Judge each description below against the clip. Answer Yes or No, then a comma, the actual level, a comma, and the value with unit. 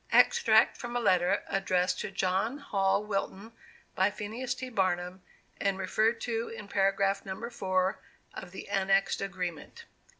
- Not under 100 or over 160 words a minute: Yes, average, 140 wpm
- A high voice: Yes, high, 195 Hz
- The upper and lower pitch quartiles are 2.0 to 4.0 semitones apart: Yes, average, 2.9 semitones